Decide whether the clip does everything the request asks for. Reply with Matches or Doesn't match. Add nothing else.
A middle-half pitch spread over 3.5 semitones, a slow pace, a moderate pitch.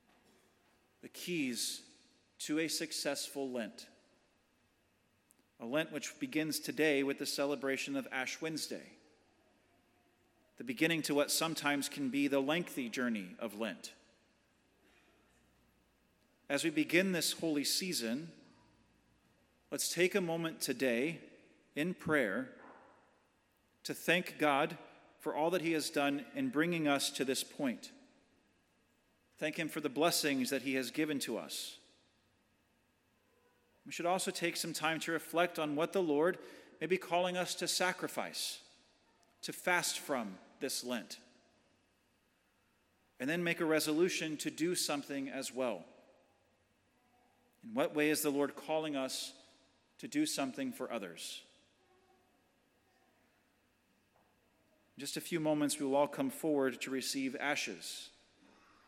Matches